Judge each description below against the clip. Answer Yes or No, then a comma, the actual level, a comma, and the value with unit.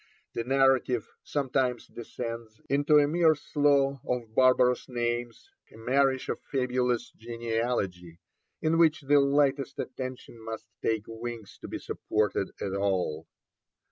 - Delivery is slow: Yes, slow, 125 wpm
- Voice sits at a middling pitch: No, low, 125 Hz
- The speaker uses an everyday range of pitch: Yes, average, 3.4 semitones